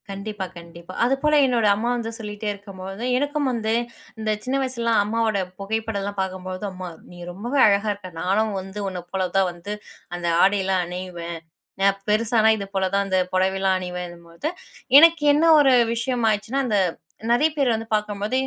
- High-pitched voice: Yes, high, 205 Hz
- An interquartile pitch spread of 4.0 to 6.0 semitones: No, average, 3.4 semitones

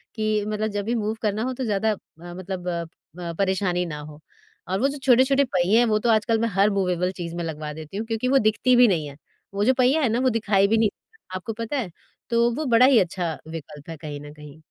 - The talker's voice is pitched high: Yes, high, 205 Hz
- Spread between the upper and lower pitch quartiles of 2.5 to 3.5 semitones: No, average, 4.9 semitones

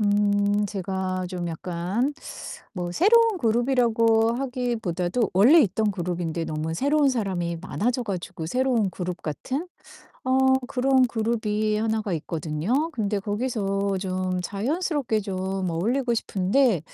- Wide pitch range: No, average, 5.0 semitones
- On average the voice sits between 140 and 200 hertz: No, high, 210 Hz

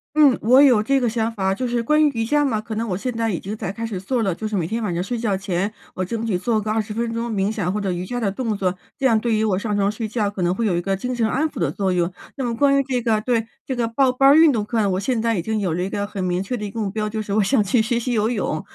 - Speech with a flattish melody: No, average, 3.4 semitones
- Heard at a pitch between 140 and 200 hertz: No, high, 220 Hz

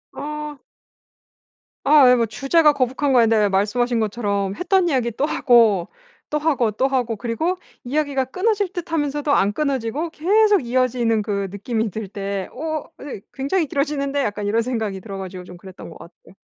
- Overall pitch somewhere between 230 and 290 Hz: Yes, very high, 250 Hz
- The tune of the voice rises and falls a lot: Yes, wide, 6.0 semitones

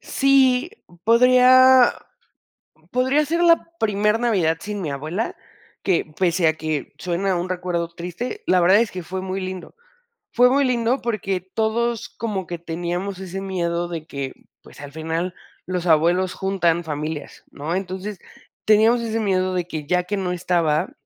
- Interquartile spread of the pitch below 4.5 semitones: No, average, 4.8 semitones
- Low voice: No, medium, 185 Hz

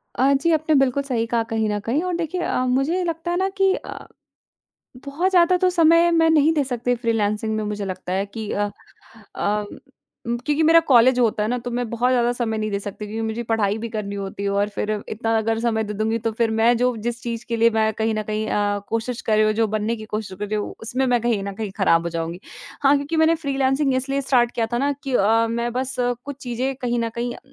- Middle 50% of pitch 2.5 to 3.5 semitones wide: No, average, 4.0 semitones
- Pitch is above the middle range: Yes, high, 235 Hz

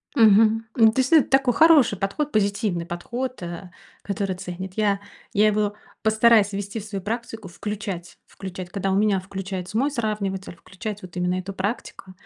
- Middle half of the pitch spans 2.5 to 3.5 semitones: Yes, average, 2.9 semitones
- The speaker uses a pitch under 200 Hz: No, high, 205 Hz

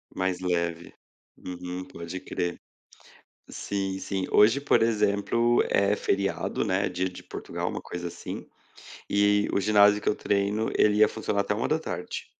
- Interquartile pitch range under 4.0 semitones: Yes, narrow, 2.4 semitones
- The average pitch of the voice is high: No, low, 100 Hz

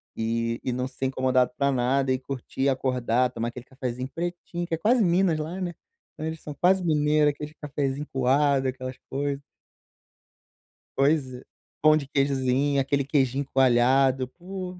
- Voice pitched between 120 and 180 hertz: Yes, medium, 140 Hz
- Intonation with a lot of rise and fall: No, average, 3.0 semitones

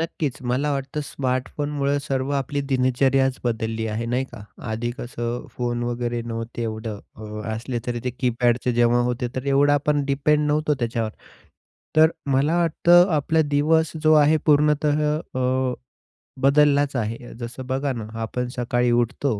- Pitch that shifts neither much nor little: Yes, average, 3.3 semitones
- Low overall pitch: Yes, low, 130 Hz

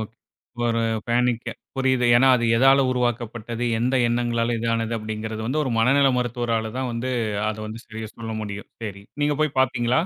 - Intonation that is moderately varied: No, narrow, 2.3 semitones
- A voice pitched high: No, low, 120 Hz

